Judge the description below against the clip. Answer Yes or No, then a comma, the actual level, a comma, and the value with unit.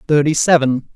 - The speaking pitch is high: No, medium, 145 Hz